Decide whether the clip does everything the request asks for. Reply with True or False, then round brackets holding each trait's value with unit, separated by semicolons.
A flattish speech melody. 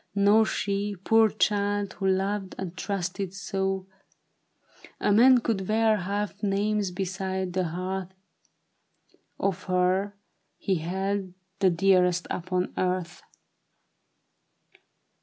True (1.7 semitones)